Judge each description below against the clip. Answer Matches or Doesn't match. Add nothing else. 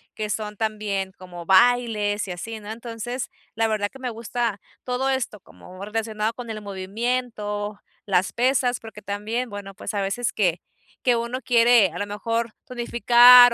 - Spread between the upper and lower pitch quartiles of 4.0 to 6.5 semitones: Doesn't match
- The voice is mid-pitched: Doesn't match